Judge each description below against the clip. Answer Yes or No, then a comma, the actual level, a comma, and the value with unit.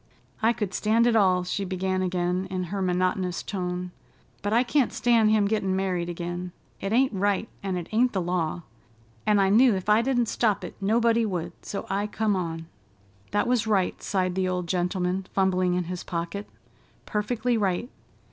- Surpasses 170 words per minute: Yes, average, 180 wpm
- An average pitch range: Yes, average, 3.1 semitones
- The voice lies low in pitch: No, high, 190 Hz